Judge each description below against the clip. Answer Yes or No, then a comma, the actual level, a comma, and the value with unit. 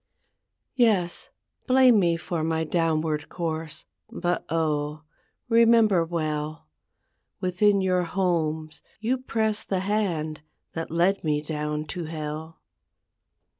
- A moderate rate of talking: No, slow, 105 wpm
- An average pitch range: Yes, average, 4.0 semitones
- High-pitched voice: No, medium, 165 Hz